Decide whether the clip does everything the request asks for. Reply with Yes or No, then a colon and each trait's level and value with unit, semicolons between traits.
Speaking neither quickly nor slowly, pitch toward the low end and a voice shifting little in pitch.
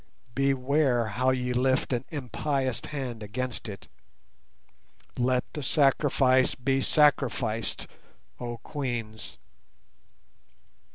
No: slow, 90 wpm; low, 130 Hz; narrow, 2.3 semitones